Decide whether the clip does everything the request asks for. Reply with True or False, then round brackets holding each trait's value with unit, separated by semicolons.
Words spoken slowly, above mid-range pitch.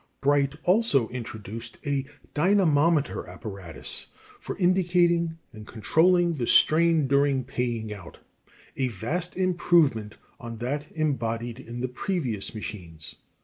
False (115 wpm; 135 Hz)